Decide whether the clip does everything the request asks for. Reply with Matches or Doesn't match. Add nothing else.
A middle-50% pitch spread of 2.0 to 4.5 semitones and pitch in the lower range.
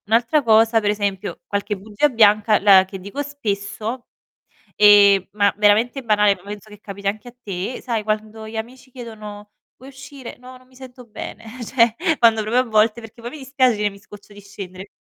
Doesn't match